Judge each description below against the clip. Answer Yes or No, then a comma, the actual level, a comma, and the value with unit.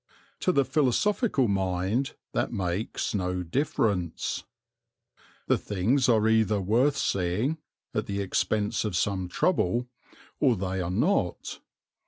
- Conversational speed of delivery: No, slow, 120 wpm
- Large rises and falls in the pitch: Yes, wide, 5.7 semitones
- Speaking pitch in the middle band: No, low, 105 Hz